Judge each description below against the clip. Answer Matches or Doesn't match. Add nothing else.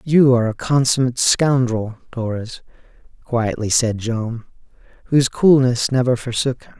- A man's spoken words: Matches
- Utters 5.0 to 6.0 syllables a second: Doesn't match